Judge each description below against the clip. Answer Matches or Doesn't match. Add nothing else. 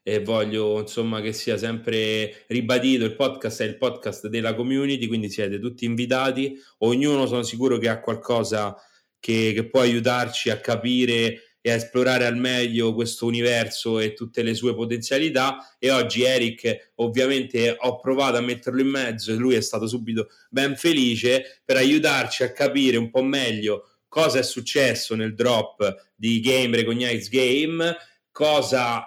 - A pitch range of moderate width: Doesn't match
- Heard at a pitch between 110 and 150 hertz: Matches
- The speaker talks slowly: Doesn't match